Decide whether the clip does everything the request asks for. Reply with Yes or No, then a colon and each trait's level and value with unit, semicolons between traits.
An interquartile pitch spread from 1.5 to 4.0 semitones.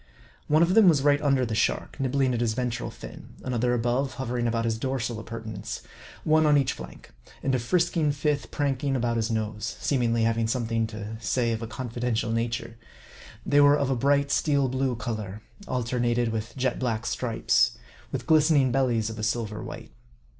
Yes: average, 3.2 semitones